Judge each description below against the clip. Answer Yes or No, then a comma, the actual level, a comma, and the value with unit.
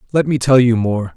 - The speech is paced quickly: Yes, fast, 260 wpm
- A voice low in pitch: Yes, low, 120 Hz